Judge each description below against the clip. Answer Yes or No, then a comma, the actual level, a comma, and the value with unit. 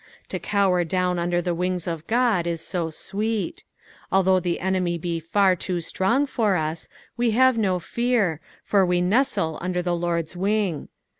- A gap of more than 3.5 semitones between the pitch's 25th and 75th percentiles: No, average, 3.0 semitones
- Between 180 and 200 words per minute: No, average, 165 wpm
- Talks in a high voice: No, medium, 180 Hz